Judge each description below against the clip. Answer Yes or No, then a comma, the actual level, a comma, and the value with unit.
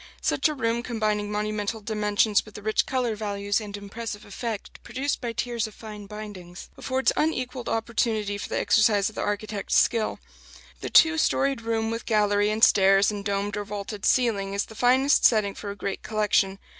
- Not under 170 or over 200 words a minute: Yes, average, 180 wpm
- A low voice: No, high, 215 Hz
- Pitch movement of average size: No, narrow, 2.3 semitones